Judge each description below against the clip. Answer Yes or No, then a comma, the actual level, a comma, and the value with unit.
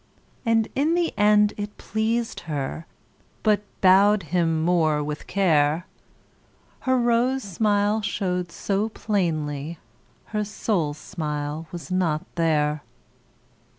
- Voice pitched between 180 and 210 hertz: Yes, medium, 185 Hz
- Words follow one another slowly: Yes, slow, 110 wpm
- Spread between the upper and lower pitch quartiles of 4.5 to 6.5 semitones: Yes, average, 5.1 semitones